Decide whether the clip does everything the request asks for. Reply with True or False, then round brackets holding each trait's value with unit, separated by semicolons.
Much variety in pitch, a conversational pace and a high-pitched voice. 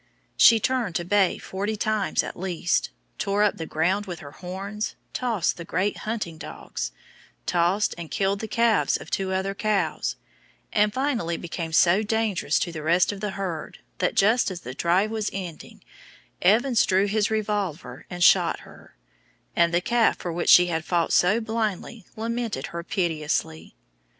False (3.8 semitones; 155 wpm; 195 Hz)